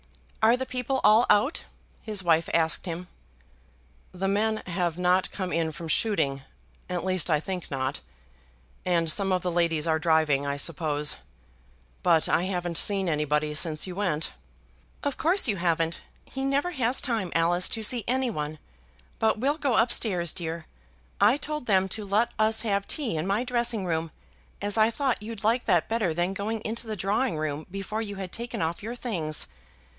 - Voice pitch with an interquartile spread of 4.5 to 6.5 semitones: Yes, average, 5.2 semitones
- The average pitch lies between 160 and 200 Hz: Yes, high, 190 Hz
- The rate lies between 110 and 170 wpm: No, average, 180 wpm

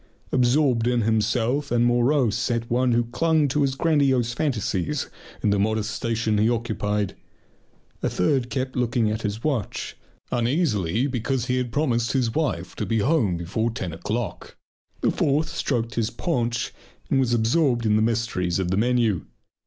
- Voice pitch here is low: Yes, low, 120 Hz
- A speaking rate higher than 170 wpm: No, average, 160 wpm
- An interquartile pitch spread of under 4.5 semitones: Yes, average, 3.0 semitones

